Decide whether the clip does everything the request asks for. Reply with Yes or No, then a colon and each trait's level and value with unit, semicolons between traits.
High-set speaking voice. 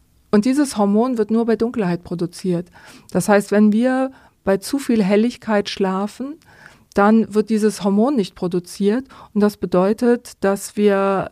Yes: high, 210 Hz